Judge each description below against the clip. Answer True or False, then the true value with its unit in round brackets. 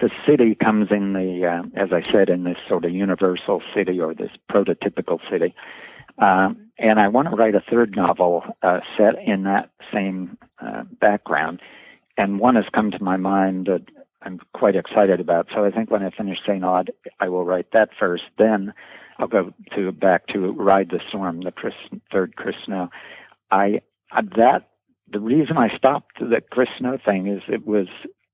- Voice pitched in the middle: False (100 Hz)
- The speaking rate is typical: True (185 wpm)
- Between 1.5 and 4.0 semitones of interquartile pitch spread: True (2.7 semitones)